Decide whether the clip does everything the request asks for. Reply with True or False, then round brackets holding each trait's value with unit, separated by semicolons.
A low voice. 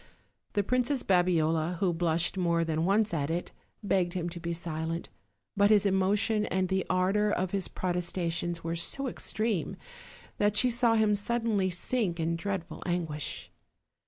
False (185 Hz)